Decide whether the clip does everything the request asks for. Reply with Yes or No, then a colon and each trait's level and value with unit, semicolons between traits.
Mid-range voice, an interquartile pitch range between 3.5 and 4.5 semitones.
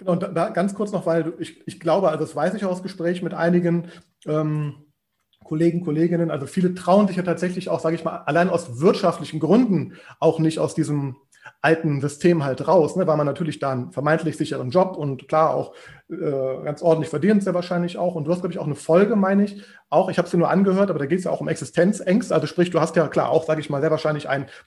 No: medium, 165 Hz; average, 2.8 semitones